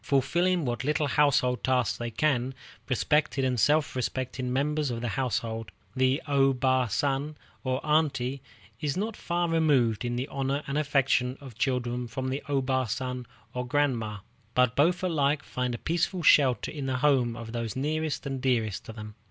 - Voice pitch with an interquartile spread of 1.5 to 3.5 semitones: Yes, average, 2.9 semitones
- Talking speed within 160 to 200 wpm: Yes, average, 175 wpm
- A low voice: Yes, low, 130 Hz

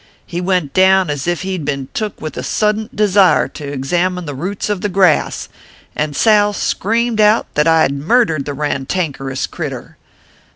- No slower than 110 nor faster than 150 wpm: No, average, 175 wpm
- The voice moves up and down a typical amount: No, wide, 5.8 semitones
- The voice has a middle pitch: Yes, medium, 180 Hz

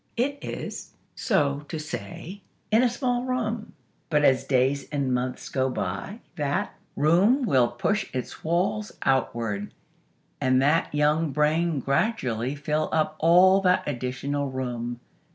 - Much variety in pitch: Yes, wide, 6.3 semitones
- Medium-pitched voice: Yes, medium, 150 Hz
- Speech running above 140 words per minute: No, slow, 135 wpm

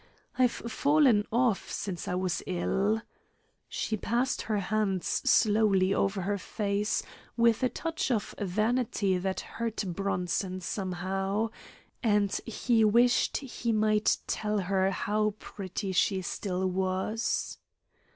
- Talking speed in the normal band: No, slow, 120 wpm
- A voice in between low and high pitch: No, high, 205 Hz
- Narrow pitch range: No, average, 3.0 semitones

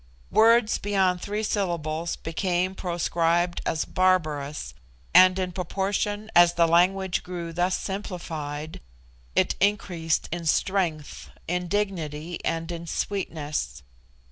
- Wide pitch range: No, average, 2.8 semitones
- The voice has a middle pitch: Yes, medium, 175 Hz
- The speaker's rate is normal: No, slow, 110 wpm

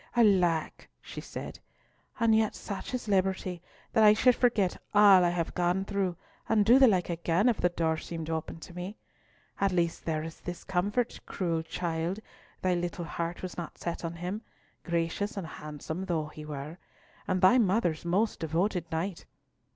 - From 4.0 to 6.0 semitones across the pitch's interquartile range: No, average, 3.3 semitones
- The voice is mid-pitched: Yes, medium, 180 Hz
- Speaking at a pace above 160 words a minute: Yes, average, 170 wpm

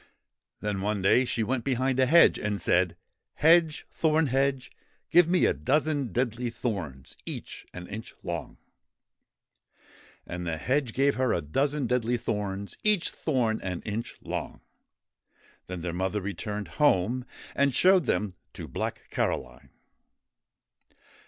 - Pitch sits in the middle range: No, low, 115 Hz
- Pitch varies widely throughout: Yes, wide, 6.2 semitones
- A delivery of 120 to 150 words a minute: Yes, average, 145 wpm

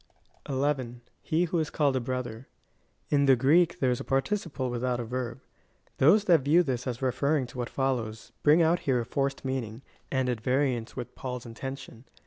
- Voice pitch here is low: Yes, low, 130 Hz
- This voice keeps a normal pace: Yes, average, 195 wpm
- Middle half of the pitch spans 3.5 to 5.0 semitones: No, average, 2.8 semitones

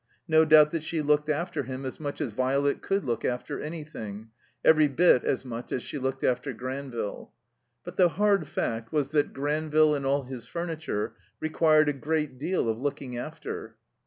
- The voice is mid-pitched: Yes, medium, 145 Hz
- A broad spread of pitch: No, average, 3.3 semitones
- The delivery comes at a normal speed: Yes, average, 180 wpm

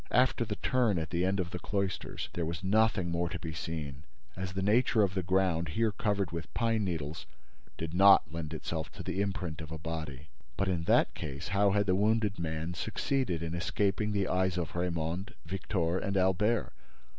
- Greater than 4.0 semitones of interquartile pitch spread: No, average, 3.5 semitones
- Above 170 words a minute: Yes, average, 195 wpm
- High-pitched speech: No, very low, 90 Hz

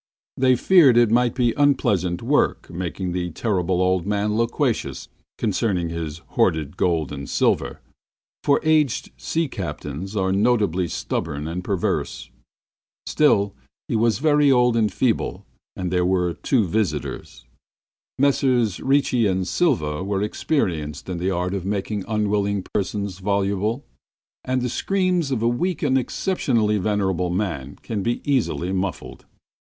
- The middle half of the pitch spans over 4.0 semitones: Yes, average, 5.2 semitones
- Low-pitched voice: Yes, low, 105 Hz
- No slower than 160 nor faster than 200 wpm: No, average, 140 wpm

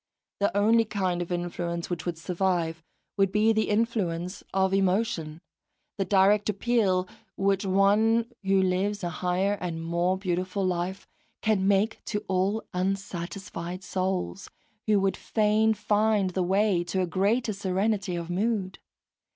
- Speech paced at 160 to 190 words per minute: No, average, 140 wpm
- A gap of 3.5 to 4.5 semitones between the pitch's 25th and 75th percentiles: No, narrow, 2.4 semitones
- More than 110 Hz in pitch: Yes, high, 190 Hz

